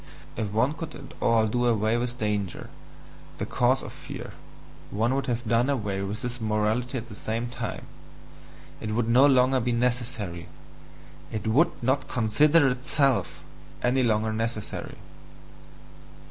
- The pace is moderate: Yes, average, 145 wpm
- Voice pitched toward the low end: Yes, low, 120 Hz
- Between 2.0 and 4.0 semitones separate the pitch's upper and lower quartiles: Yes, average, 2.8 semitones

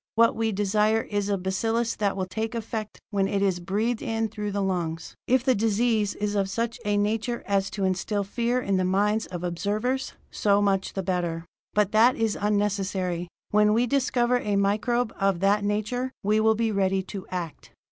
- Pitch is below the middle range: No, high, 205 Hz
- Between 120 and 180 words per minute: No, average, 190 wpm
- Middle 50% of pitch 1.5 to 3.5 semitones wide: Yes, narrow, 2.5 semitones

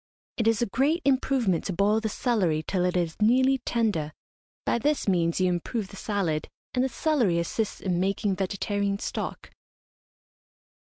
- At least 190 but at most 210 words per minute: No, average, 160 wpm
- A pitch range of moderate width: Yes, average, 4.8 semitones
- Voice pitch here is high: Yes, high, 200 Hz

